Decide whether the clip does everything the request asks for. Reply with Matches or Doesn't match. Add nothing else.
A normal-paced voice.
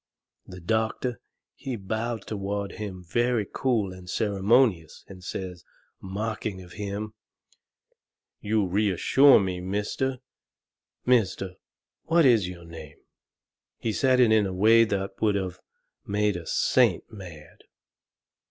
Doesn't match